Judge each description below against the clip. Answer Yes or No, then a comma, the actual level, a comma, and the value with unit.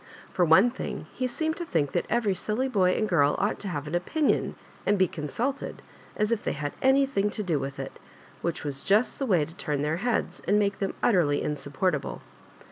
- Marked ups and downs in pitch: Yes, wide, 7.3 semitones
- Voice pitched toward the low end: No, high, 190 Hz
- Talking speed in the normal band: No, fast, 210 wpm